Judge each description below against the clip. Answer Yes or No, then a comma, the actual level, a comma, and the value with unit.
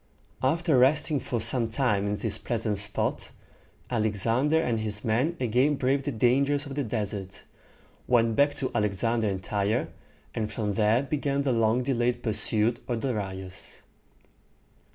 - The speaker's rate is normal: Yes, average, 145 wpm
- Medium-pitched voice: No, low, 115 Hz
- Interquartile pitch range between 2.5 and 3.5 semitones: No, average, 4.1 semitones